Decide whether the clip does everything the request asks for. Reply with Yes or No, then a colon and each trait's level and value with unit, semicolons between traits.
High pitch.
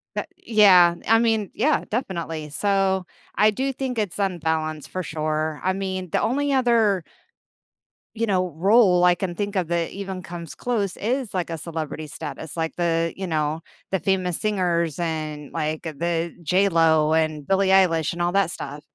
No: medium, 180 Hz